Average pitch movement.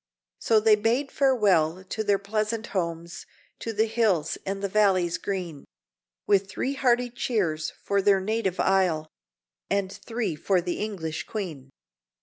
Yes: average, 3.9 semitones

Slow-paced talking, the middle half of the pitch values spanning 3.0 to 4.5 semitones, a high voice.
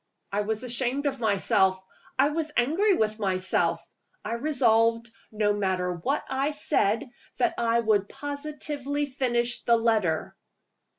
No: slow, 130 wpm; average, 5.3 semitones; high, 235 Hz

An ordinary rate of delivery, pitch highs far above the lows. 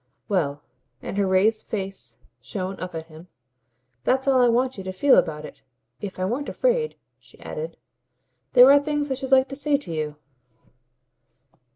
Yes: average, 175 wpm; wide, 6.8 semitones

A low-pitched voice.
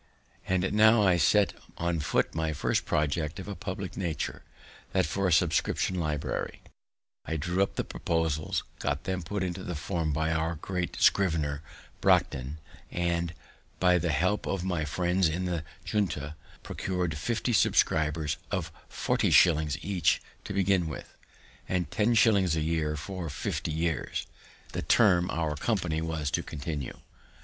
Yes: very low, 85 Hz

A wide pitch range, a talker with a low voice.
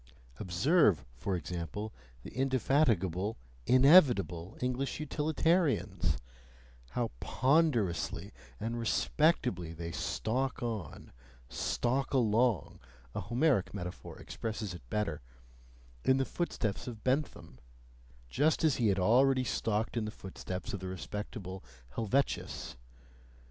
Yes: wide, 6.2 semitones; low, 110 Hz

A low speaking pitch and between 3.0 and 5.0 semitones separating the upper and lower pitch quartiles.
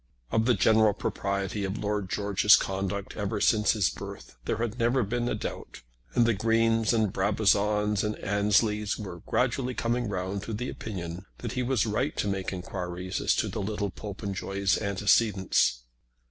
No: low, 105 Hz; narrow, 2.5 semitones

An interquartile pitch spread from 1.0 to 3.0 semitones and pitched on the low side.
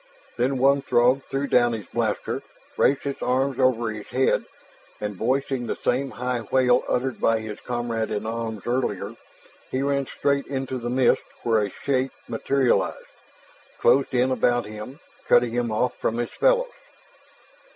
Yes: narrow, 2.5 semitones; low, 125 Hz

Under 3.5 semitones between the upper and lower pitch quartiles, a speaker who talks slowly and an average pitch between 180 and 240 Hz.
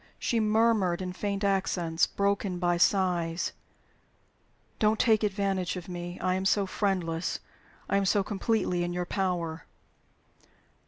Yes: narrow, 2.4 semitones; slow, 130 wpm; high, 190 Hz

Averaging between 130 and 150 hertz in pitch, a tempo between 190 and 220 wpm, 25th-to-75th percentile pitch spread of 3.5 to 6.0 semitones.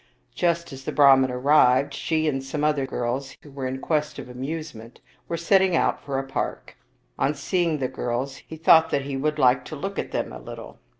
No: medium, 140 Hz; fast, 205 wpm; average, 2.8 semitones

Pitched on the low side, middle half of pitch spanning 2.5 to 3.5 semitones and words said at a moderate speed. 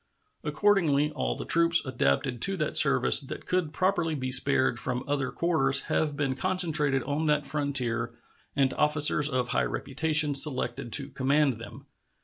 No: medium, 145 Hz; average, 2.8 semitones; average, 150 wpm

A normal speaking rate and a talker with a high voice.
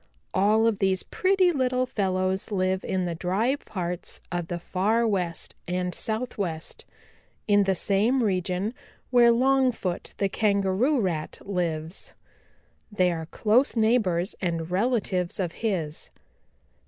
No: slow, 125 wpm; high, 195 Hz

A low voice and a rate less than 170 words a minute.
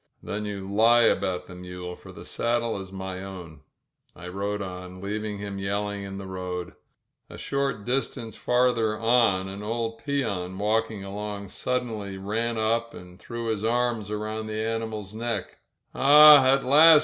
Yes: low, 105 Hz; average, 160 wpm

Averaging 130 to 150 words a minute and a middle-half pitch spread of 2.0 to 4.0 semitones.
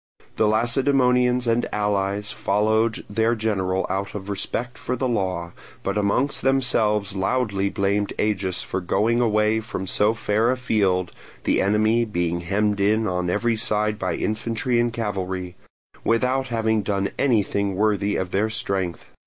Yes: average, 145 wpm; average, 2.8 semitones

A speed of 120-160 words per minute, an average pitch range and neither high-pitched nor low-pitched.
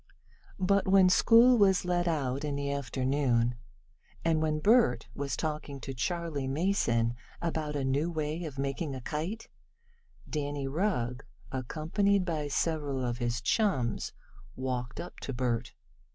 Yes: average, 140 wpm; average, 4.8 semitones; medium, 145 Hz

